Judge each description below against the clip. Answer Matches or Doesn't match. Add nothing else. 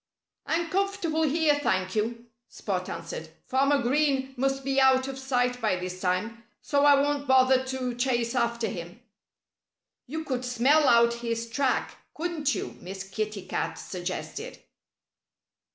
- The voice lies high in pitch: Matches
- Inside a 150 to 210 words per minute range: Doesn't match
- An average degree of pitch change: Matches